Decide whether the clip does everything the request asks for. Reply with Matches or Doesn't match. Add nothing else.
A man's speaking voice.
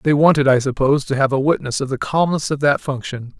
Matches